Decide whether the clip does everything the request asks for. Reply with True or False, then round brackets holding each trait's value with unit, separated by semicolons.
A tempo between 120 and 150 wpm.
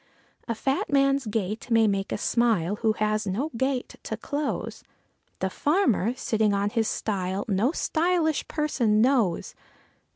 True (140 wpm)